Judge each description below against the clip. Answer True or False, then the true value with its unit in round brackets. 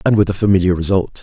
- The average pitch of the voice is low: True (95 Hz)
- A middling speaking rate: False (245 wpm)